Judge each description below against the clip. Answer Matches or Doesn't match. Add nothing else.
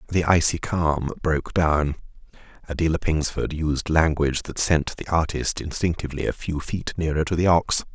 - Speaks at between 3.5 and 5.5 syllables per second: Matches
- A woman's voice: Doesn't match